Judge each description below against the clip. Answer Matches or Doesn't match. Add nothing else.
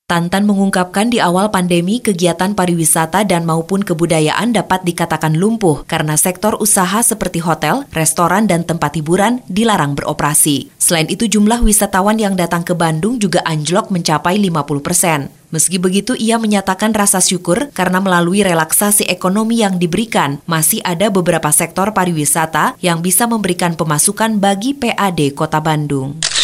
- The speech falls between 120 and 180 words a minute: Matches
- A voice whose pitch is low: Doesn't match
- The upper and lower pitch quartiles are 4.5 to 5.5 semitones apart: Doesn't match